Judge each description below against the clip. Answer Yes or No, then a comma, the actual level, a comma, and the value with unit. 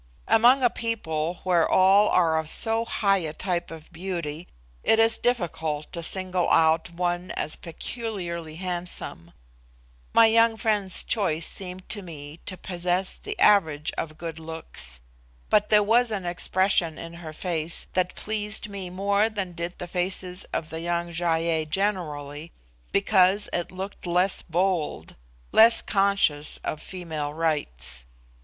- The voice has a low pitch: No, medium, 180 Hz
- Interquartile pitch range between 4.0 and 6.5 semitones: No, average, 3.6 semitones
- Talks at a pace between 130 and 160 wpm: Yes, average, 145 wpm